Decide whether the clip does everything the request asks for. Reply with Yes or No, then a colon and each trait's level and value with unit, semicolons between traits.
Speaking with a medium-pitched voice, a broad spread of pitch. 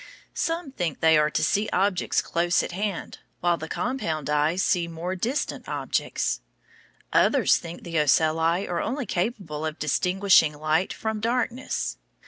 No: medium, 175 Hz; average, 4.7 semitones